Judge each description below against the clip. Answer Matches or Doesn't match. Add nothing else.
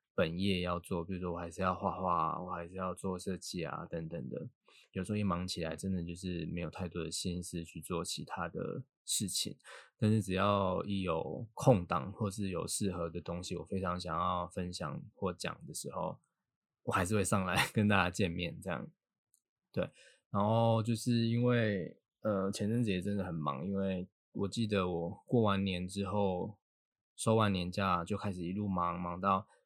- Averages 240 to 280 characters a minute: Matches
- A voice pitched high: Doesn't match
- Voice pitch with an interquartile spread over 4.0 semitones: Doesn't match